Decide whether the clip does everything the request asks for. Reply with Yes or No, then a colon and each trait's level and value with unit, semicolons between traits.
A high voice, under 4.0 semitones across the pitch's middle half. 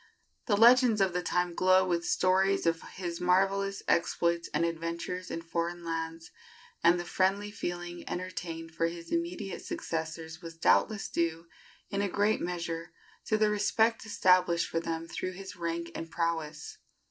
No: medium, 175 Hz; narrow, 2.6 semitones